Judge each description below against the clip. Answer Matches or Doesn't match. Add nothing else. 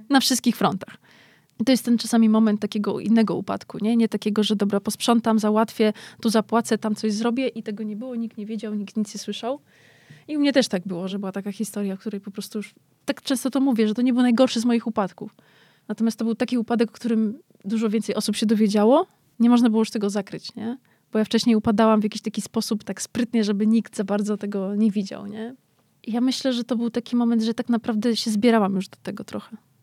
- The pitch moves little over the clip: Matches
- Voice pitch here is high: Matches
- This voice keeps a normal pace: Doesn't match